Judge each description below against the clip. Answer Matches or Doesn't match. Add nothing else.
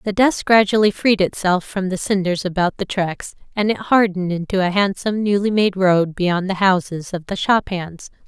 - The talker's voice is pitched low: Doesn't match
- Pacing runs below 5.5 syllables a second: Matches